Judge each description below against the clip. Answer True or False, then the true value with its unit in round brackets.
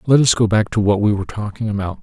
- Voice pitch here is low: True (105 Hz)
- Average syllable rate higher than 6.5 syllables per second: True (6.9 syllables/s)